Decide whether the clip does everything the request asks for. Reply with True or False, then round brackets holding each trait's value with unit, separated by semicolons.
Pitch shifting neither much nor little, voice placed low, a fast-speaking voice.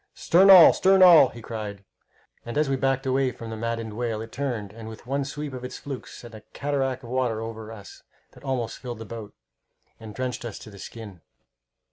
True (3.3 semitones; 120 Hz; 210 wpm)